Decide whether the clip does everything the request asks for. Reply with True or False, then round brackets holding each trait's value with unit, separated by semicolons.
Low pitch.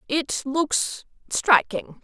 False (270 Hz)